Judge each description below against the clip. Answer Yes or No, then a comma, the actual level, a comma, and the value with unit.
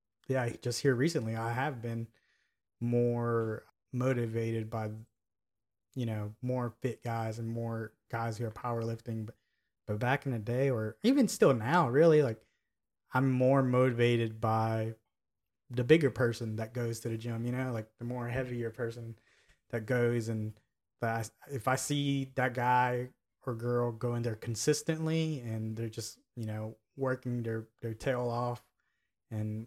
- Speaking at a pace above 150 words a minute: Yes, average, 160 wpm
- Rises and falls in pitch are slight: Yes, narrow, 2.3 semitones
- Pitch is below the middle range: Yes, low, 120 Hz